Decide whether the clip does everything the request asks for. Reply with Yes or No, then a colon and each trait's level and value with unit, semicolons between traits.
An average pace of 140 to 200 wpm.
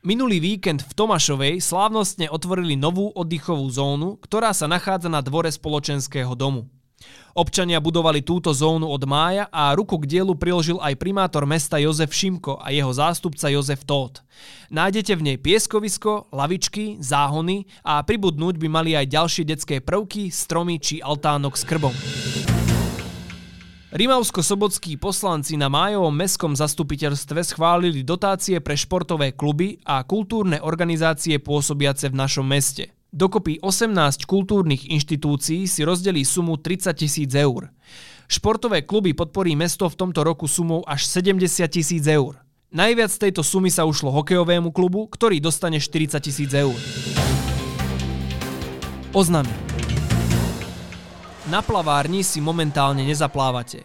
No: average, 130 wpm